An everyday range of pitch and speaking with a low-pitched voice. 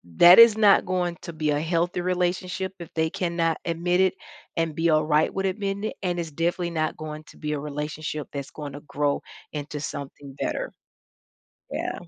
No: average, 3.0 semitones; medium, 165 Hz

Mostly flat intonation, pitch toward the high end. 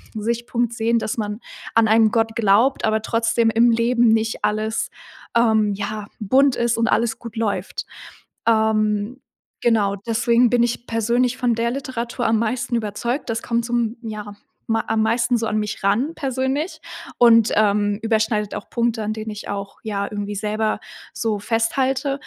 Yes: narrow, 1.8 semitones; high, 225 Hz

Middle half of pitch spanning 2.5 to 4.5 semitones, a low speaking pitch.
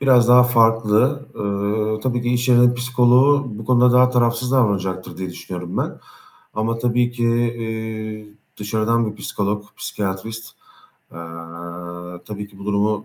Yes: average, 2.8 semitones; low, 115 Hz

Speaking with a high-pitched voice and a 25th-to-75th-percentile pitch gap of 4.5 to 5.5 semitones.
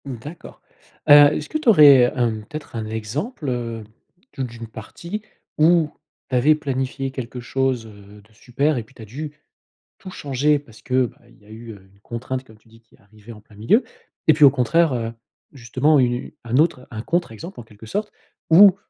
No: low, 125 Hz; average, 4.8 semitones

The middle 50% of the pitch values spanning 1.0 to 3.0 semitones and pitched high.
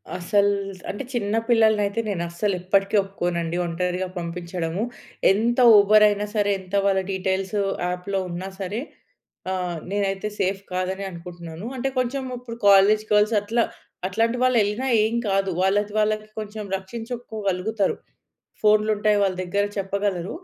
Yes: narrow, 2.5 semitones; high, 200 Hz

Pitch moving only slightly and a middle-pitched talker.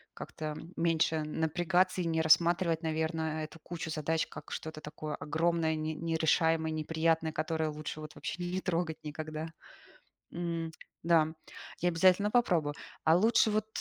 Yes: narrow, 1.6 semitones; medium, 160 Hz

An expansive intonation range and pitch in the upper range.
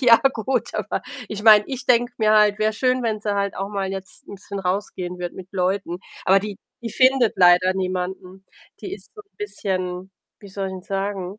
No: average, 2.8 semitones; high, 200 Hz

